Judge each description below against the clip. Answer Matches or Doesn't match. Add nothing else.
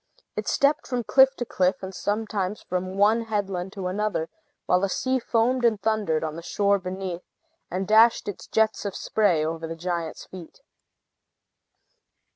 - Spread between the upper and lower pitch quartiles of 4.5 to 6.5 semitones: Doesn't match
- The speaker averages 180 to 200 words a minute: Doesn't match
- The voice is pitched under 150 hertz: Doesn't match